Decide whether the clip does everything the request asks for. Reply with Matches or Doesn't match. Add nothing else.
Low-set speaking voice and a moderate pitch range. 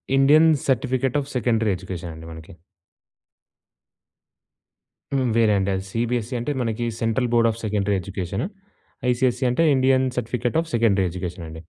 Matches